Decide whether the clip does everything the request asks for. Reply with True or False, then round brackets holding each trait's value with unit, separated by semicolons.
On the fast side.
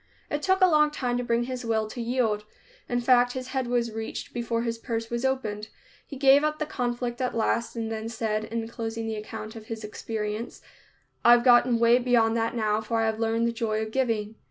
True (220 wpm)